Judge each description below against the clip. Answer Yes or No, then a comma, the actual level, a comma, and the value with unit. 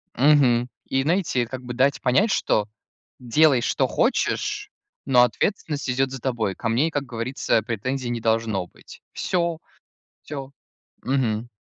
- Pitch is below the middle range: Yes, low, 130 Hz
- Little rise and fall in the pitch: No, average, 3.1 semitones